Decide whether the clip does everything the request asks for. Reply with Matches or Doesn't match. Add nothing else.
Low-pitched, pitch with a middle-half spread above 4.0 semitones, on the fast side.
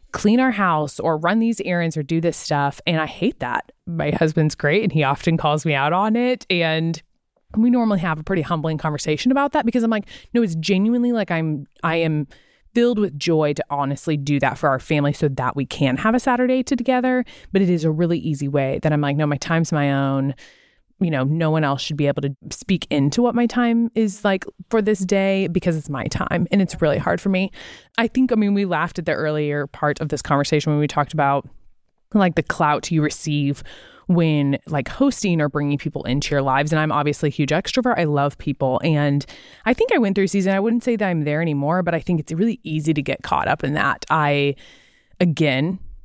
Doesn't match